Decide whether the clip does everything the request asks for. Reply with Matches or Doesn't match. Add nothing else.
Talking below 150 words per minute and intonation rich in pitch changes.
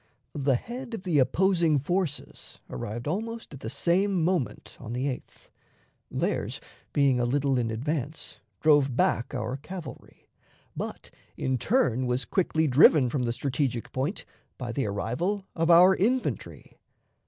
Matches